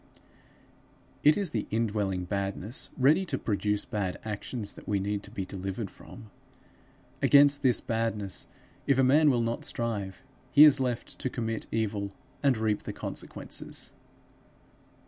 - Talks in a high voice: No, low, 110 Hz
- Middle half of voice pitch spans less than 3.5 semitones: No, average, 4.2 semitones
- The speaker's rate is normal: Yes, average, 145 wpm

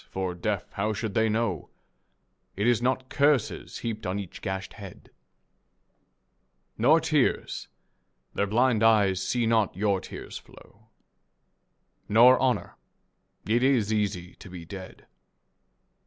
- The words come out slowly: Yes, slow, 125 wpm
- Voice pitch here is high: No, low, 110 Hz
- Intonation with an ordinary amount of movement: Yes, average, 3.7 semitones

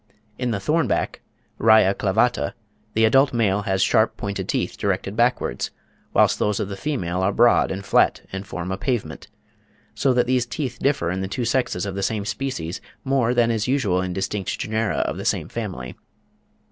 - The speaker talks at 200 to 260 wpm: No, average, 185 wpm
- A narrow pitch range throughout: No, average, 4.3 semitones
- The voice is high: No, low, 105 Hz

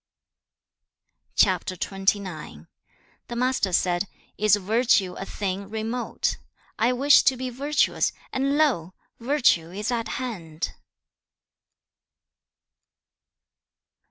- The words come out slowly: Yes, slow, 90 wpm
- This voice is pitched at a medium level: No, high, 215 Hz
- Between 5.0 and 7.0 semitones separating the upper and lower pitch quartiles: Yes, average, 5.3 semitones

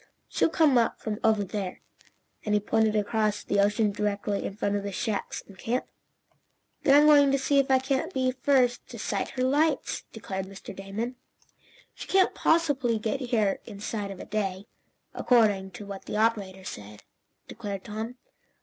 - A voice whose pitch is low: No, high, 215 Hz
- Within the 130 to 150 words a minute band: No, average, 175 wpm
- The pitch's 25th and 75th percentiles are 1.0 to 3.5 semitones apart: No, average, 4.3 semitones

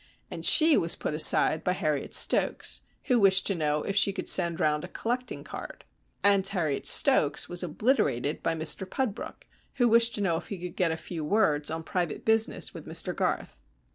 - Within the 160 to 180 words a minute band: No, average, 195 wpm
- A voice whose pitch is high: No, medium, 180 Hz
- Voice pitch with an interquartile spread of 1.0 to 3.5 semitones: No, average, 5.2 semitones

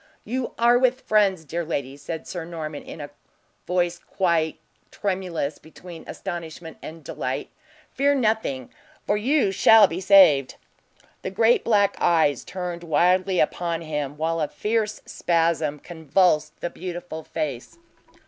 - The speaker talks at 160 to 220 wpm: No, slow, 135 wpm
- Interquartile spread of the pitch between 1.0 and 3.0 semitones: No, average, 3.8 semitones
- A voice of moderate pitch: Yes, medium, 175 Hz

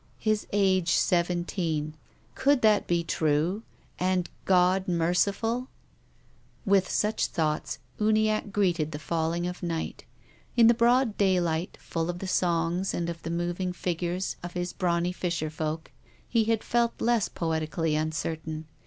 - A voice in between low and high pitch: Yes, medium, 175 Hz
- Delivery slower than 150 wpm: Yes, average, 140 wpm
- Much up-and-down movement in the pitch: No, average, 3.4 semitones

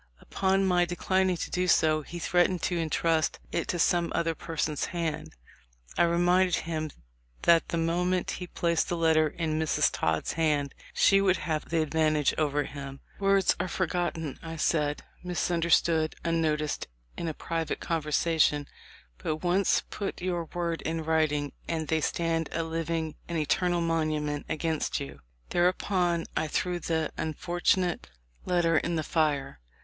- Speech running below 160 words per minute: Yes, average, 150 wpm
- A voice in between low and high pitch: Yes, medium, 165 Hz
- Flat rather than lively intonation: Yes, narrow, 2.1 semitones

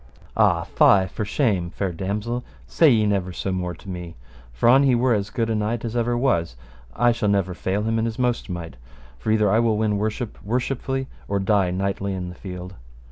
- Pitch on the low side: Yes, low, 105 Hz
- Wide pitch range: No, average, 3.9 semitones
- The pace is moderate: No, fast, 210 wpm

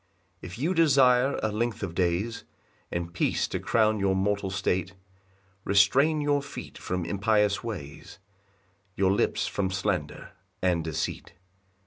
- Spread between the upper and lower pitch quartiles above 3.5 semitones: Yes, average, 4.2 semitones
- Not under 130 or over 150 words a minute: Yes, slow, 135 wpm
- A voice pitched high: No, low, 100 Hz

